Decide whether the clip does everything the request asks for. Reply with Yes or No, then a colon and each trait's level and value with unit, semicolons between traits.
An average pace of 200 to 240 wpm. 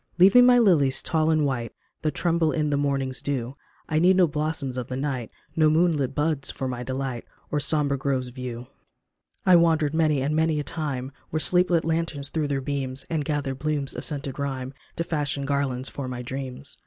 Yes: fast, 205 wpm